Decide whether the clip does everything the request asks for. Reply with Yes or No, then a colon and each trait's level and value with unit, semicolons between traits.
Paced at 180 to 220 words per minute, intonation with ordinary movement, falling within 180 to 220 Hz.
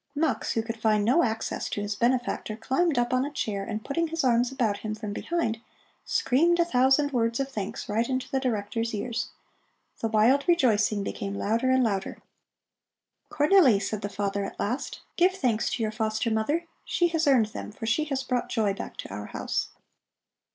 No: average, 190 wpm; average, 4.2 semitones; high, 235 Hz